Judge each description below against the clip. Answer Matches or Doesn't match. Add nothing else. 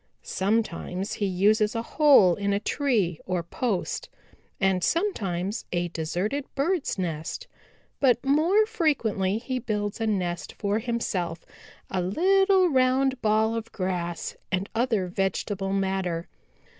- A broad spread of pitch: Matches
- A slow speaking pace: Matches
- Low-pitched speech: Doesn't match